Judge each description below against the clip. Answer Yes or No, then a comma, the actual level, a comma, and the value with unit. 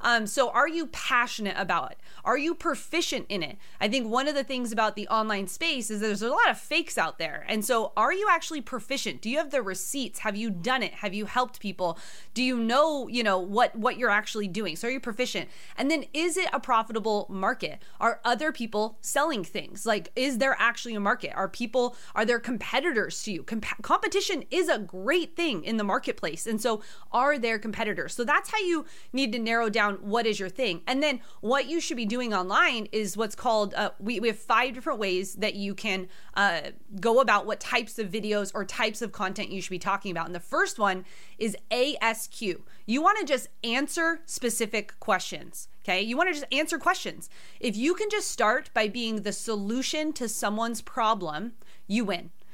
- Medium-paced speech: No, fast, 210 wpm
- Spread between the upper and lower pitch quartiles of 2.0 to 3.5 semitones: No, average, 4.4 semitones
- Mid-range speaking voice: No, high, 230 Hz